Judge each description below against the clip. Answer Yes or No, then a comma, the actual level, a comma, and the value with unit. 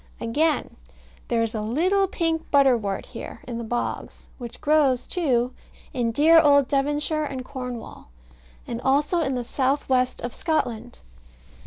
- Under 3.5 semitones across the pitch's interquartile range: No, average, 4.2 semitones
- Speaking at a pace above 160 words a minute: No, average, 145 wpm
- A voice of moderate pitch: No, very high, 265 Hz